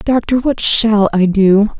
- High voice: Yes, high, 215 Hz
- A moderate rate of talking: Yes, average, 165 wpm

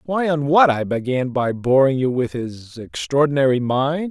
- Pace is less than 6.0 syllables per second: Yes, 4.4 syllables/s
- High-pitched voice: No, medium, 140 Hz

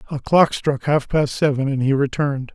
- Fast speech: Yes, fast, 210 wpm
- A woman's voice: No, male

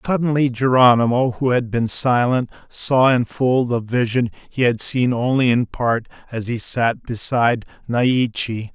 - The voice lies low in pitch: Yes, low, 120 Hz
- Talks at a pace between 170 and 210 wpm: No, average, 150 wpm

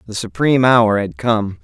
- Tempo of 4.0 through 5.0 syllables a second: Yes, 4.8 syllables/s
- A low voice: Yes, low, 110 Hz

